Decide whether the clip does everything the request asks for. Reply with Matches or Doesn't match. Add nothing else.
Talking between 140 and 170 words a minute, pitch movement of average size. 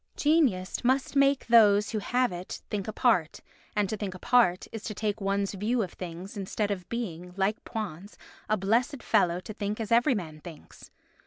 Doesn't match